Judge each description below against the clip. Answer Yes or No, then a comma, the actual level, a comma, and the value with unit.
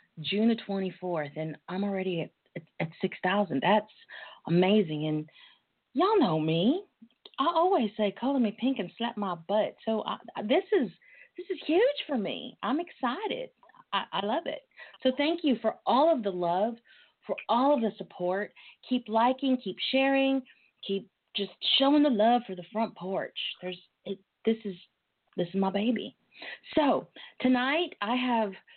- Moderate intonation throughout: No, wide, 6.0 semitones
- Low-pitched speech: No, high, 220 Hz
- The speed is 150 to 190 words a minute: Yes, average, 170 wpm